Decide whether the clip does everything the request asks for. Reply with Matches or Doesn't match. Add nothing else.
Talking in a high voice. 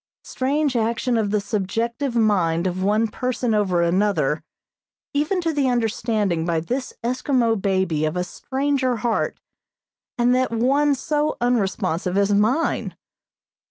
Matches